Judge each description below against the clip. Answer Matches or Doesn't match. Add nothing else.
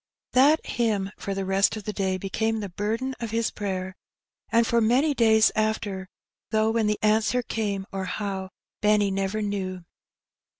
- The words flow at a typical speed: Matches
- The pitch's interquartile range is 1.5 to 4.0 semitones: Matches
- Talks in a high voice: Matches